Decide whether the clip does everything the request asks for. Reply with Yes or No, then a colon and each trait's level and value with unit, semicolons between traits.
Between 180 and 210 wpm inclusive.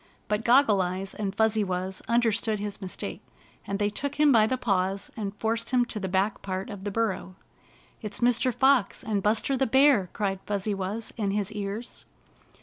Yes: average, 190 wpm